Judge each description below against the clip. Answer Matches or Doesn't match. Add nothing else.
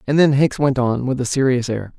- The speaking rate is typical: Doesn't match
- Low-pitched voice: Matches